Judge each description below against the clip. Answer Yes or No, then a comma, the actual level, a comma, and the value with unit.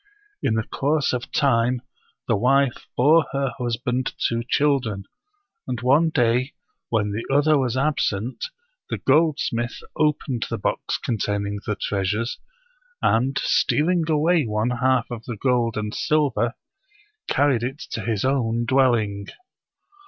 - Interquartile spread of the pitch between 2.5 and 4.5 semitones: Yes, average, 3.6 semitones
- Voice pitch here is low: Yes, low, 125 Hz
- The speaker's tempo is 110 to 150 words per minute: Yes, average, 140 wpm